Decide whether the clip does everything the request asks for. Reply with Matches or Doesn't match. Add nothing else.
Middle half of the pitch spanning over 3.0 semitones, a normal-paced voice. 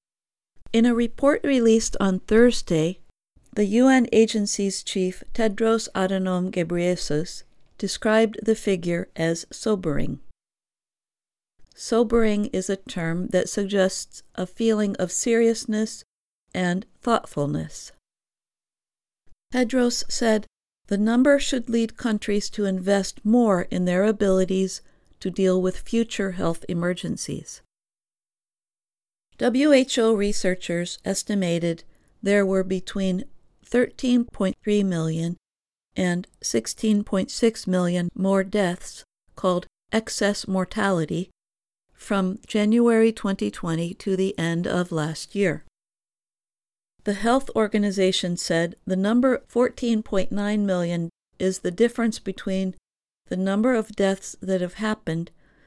Doesn't match